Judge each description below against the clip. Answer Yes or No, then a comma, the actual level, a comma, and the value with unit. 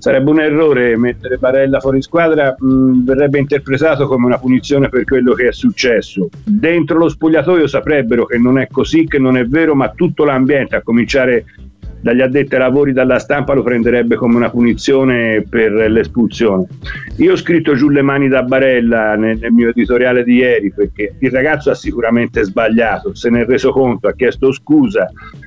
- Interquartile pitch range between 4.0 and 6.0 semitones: No, average, 3.0 semitones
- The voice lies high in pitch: No, low, 130 Hz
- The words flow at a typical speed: No, fast, 180 wpm